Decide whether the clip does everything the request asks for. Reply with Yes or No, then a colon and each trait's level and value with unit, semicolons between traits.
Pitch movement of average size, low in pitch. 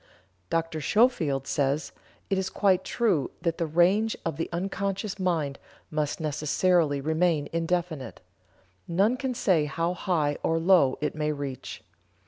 No: average, 3.8 semitones; medium, 165 Hz